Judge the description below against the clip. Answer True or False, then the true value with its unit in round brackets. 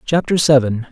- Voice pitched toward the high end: False (140 Hz)